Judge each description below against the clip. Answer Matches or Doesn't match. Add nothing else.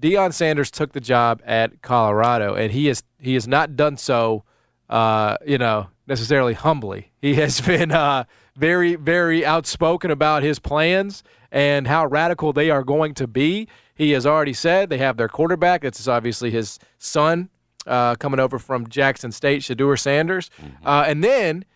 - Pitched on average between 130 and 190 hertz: Matches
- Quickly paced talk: Doesn't match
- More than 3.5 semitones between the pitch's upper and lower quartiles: Matches